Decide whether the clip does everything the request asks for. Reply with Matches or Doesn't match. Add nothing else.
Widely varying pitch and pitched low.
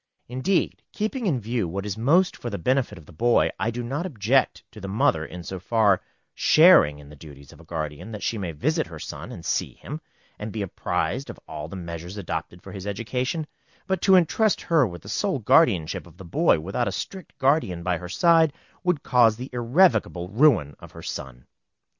Matches